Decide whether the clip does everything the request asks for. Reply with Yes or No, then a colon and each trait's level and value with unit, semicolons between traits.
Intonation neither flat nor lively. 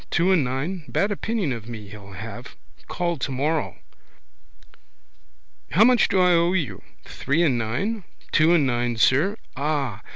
No: wide, 7.0 semitones